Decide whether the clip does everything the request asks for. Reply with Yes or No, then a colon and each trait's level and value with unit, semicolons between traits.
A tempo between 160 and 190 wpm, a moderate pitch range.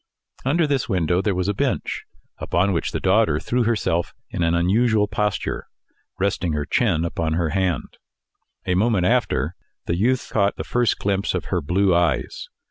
Yes: average, 170 wpm; average, 3.8 semitones